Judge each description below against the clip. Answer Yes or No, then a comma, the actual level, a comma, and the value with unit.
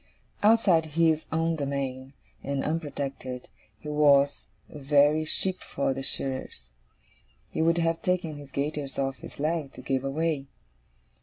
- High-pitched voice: No, medium, 145 Hz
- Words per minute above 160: No, average, 140 wpm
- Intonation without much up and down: No, average, 3.0 semitones